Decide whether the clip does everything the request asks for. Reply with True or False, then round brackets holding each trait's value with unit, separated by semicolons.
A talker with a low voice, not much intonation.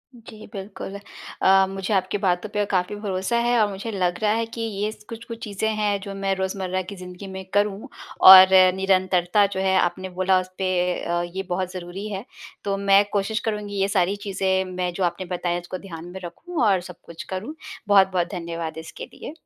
False (190 Hz; 1.9 semitones)